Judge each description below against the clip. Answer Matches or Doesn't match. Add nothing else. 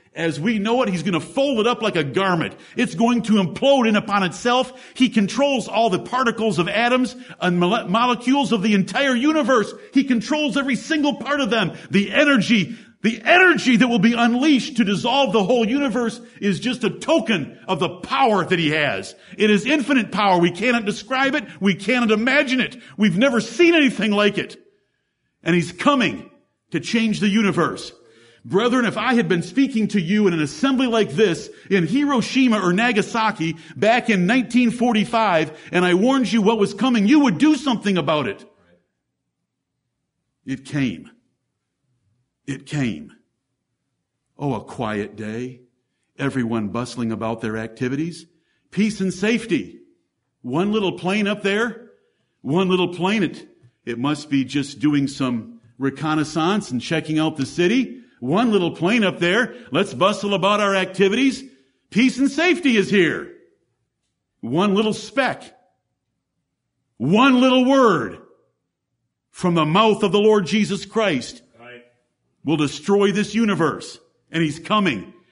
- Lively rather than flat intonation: Matches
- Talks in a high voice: Matches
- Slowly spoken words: Doesn't match